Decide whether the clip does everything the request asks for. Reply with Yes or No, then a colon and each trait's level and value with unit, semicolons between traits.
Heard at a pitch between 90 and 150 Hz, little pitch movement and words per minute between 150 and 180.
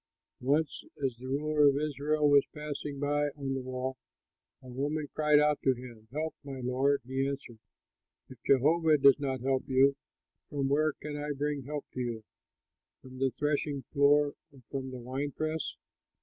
Yes: medium, 140 Hz; narrow, 2.1 semitones; average, 170 wpm